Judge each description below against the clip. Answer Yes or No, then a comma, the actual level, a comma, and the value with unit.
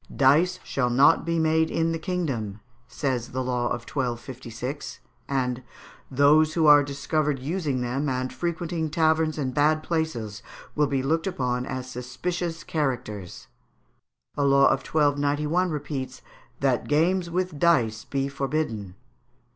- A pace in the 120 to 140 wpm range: Yes, slow, 135 wpm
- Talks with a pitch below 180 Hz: Yes, medium, 140 Hz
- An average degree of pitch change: Yes, average, 3.9 semitones